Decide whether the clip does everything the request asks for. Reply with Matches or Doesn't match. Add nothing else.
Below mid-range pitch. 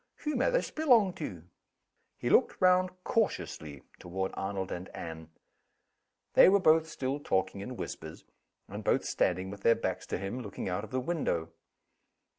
Matches